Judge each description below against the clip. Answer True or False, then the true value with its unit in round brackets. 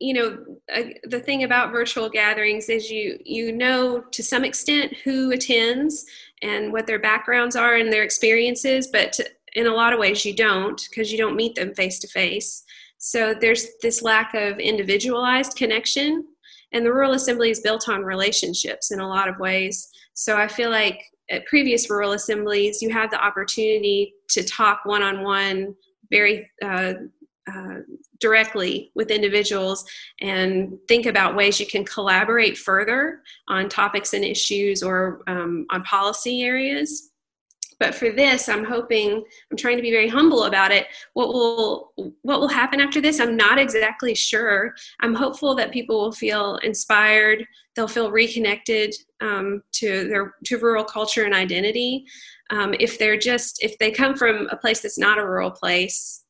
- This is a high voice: True (225 Hz)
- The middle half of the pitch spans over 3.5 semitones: False (3.1 semitones)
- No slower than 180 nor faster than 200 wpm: False (170 wpm)